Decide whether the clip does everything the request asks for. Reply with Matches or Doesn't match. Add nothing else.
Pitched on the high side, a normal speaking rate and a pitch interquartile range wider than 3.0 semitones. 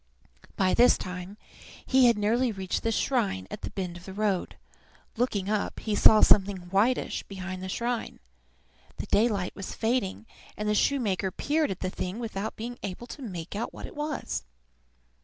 Matches